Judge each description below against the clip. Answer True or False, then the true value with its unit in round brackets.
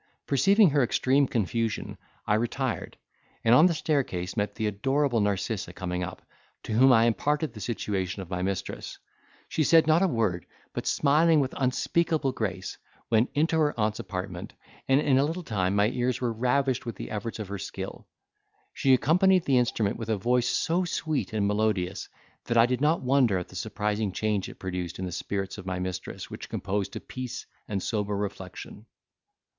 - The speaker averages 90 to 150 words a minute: False (185 wpm)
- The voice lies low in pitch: True (115 Hz)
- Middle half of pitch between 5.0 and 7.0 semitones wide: True (5.5 semitones)